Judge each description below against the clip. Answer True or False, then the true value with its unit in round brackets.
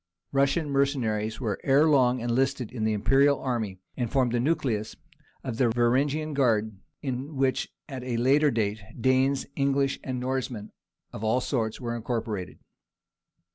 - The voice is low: True (125 Hz)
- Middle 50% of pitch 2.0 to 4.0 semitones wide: True (3.2 semitones)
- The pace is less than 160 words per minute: True (145 wpm)